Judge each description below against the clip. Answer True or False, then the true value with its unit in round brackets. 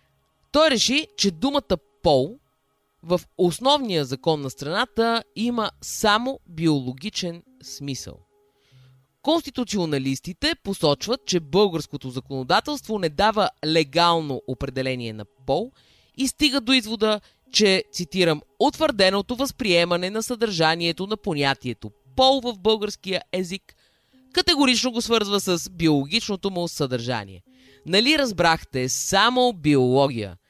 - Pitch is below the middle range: False (180 Hz)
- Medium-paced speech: False (100 wpm)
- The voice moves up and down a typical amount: False (8.8 semitones)